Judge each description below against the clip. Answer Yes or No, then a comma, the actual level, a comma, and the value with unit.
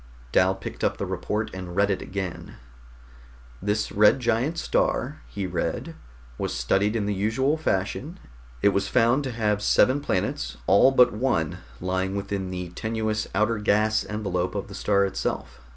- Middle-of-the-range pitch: No, low, 105 Hz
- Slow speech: No, average, 160 wpm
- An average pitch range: Yes, average, 3.0 semitones